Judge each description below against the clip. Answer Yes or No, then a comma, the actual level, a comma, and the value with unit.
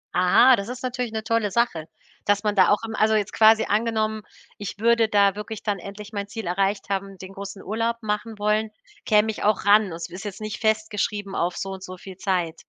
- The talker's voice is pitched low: No, high, 210 Hz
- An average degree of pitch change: No, narrow, 2.0 semitones